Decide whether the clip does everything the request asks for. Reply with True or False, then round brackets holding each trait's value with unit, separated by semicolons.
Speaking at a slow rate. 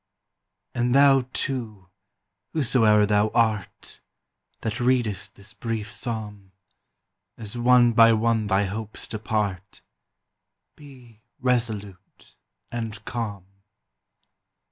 True (90 wpm)